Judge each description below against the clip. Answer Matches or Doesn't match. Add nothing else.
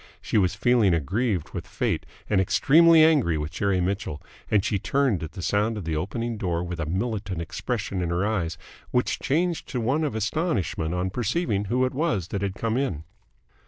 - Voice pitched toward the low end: Matches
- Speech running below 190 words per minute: Doesn't match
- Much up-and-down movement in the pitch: Matches